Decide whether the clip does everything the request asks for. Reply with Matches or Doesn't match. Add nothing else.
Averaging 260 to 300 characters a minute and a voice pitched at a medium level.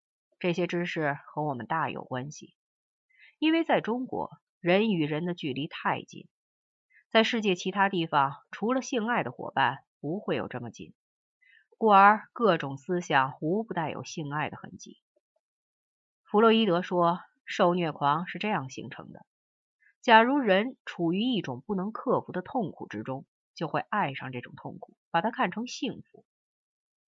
Doesn't match